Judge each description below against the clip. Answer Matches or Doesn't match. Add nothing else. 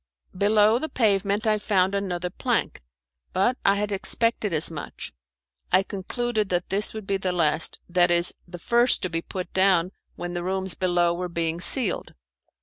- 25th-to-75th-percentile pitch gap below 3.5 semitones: Matches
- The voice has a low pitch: Doesn't match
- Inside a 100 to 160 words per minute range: Doesn't match